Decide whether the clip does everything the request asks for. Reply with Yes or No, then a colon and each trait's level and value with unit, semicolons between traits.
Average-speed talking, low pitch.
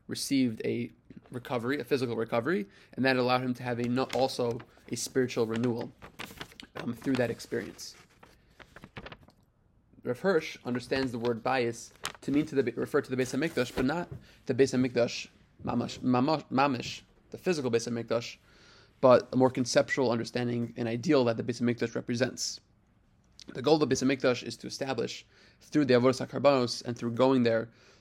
Yes: average, 165 wpm; low, 125 Hz